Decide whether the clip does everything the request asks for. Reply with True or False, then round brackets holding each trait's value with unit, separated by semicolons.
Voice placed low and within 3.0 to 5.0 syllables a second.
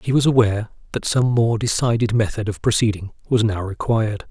False (110 Hz; 5.8 syllables/s)